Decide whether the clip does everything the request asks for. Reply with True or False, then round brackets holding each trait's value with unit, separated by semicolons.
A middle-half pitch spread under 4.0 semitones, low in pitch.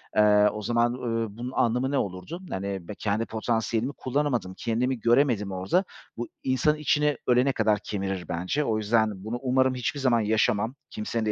True (3.6 semitones; 115 Hz)